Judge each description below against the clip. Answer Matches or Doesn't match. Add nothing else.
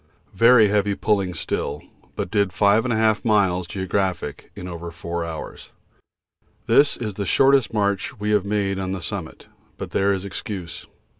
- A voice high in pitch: Doesn't match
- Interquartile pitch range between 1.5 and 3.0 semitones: Matches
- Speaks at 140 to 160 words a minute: Matches